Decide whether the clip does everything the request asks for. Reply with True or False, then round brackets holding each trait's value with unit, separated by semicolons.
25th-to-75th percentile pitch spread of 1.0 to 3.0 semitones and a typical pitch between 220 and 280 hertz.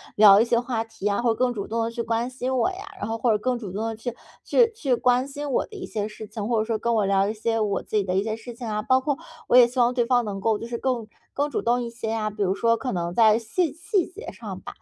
True (2.7 semitones; 230 Hz)